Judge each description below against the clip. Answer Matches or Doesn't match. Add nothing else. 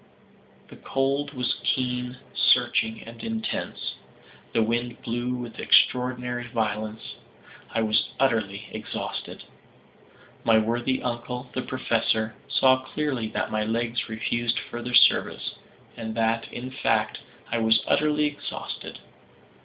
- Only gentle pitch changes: Matches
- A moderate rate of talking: Doesn't match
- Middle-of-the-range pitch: Doesn't match